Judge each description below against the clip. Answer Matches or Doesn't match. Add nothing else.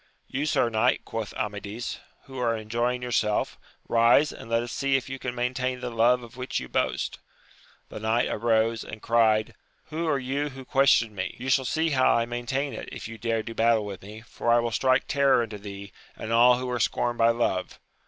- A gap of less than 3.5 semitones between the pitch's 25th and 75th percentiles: Matches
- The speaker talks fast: Matches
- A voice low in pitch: Matches